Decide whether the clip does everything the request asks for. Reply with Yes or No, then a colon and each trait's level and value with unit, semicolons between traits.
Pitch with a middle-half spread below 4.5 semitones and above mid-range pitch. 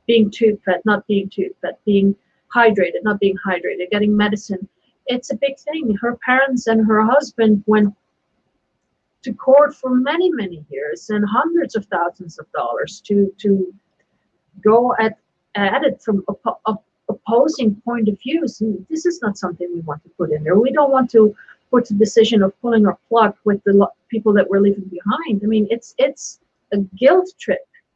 Yes: average, 3.8 semitones; high, 215 Hz